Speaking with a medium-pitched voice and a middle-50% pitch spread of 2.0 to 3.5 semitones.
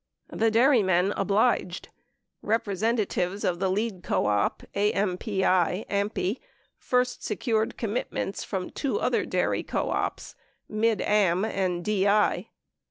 No: high, 205 Hz; average, 3.0 semitones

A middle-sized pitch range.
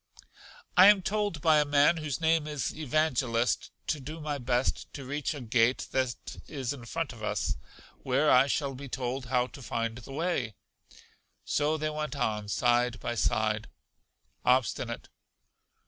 Yes: average, 4.0 semitones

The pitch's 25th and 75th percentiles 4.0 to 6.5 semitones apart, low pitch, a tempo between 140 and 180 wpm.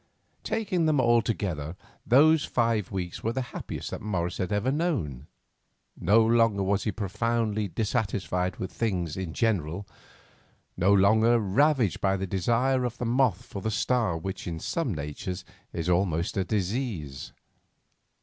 Yes: average, 4.5 semitones; low, 105 Hz; average, 150 wpm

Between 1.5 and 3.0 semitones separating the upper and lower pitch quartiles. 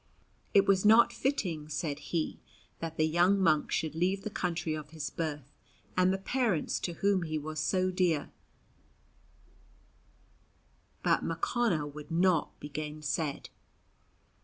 No: average, 3.5 semitones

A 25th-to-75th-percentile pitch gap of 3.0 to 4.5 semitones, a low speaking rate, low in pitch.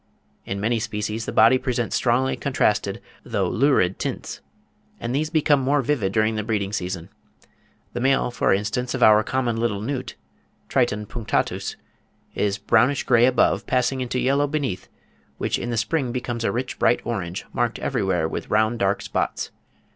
No: average, 3.6 semitones; average, 160 wpm; low, 120 Hz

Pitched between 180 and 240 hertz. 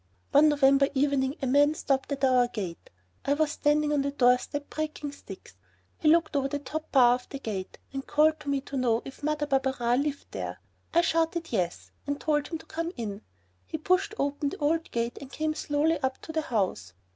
No: very high, 285 Hz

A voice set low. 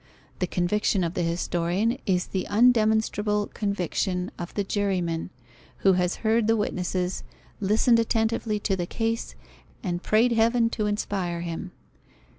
No: high, 205 Hz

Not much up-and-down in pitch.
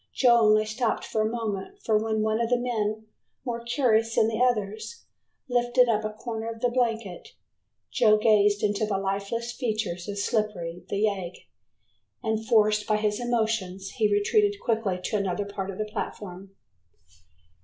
Yes: narrow, 2.2 semitones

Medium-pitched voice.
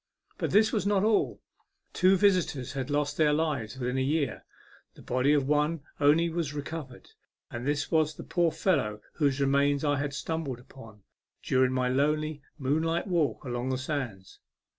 Yes: medium, 145 Hz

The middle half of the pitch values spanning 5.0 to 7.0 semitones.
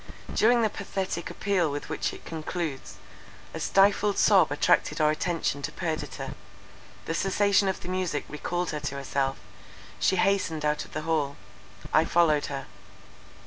No: average, 4.3 semitones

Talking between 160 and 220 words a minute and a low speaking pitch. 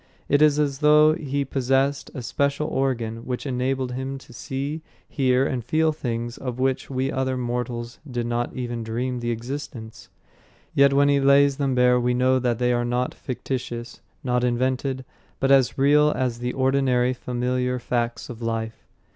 Yes: average, 170 wpm; low, 130 Hz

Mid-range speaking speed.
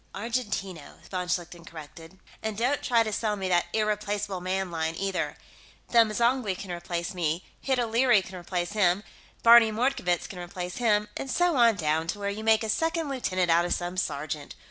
Yes: average, 185 wpm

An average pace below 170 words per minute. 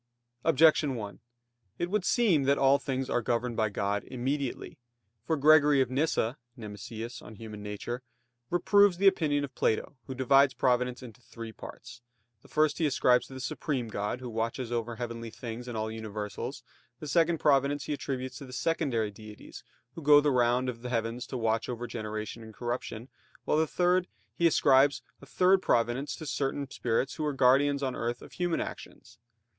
No: average, 175 wpm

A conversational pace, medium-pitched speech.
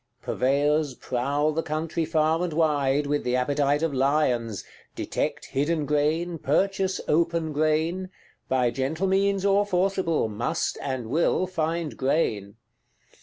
No: slow, 125 wpm; medium, 155 Hz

